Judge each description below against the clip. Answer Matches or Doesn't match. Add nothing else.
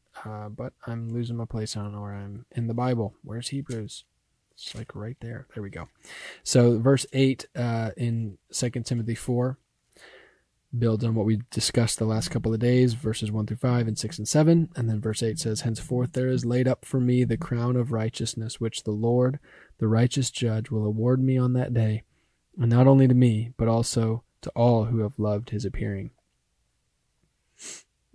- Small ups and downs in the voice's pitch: Matches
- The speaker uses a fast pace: Doesn't match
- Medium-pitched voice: Doesn't match